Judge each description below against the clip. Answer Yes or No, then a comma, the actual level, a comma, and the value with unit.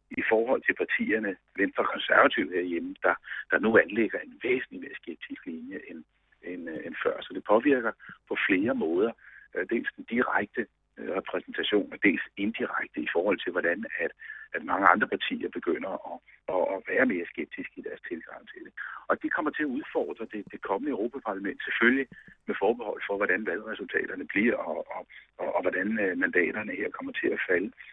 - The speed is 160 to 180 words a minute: Yes, average, 175 wpm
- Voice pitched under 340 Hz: No, very high, 390 Hz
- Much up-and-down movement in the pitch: Yes, wide, 6.4 semitones